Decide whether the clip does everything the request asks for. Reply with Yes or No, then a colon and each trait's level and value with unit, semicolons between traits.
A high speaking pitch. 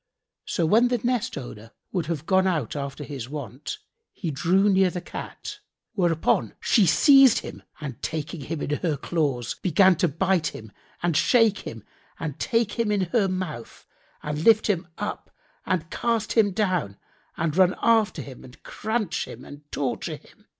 No: medium, 175 Hz